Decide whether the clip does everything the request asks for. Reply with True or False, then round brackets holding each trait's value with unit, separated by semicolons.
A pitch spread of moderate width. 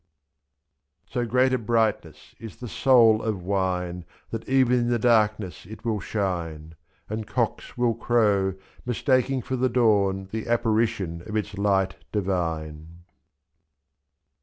True (3.8 semitones)